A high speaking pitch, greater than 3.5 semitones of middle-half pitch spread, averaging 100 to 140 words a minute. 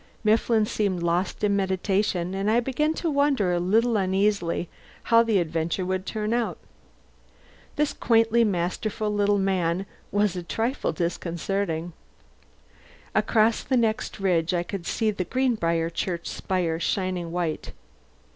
Yes: high, 195 Hz; average, 4.0 semitones; slow, 135 wpm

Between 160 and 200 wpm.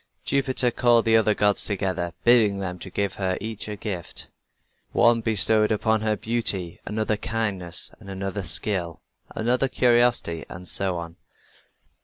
No: slow, 135 wpm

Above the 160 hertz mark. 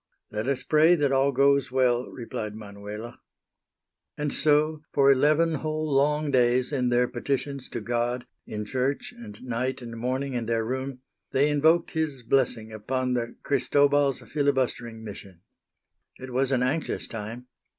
No: low, 130 Hz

